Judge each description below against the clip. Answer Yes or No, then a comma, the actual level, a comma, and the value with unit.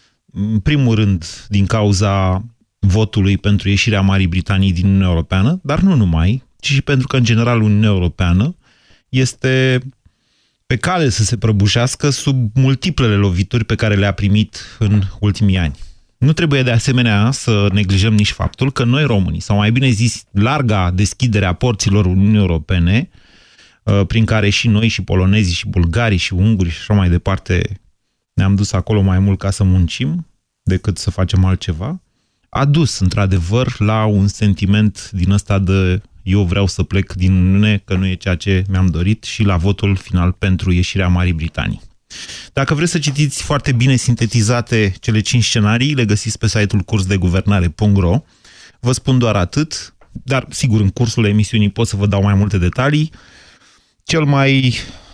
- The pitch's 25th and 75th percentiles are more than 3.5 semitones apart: Yes, average, 3.9 semitones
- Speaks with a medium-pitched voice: No, low, 105 Hz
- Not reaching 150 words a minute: No, average, 165 wpm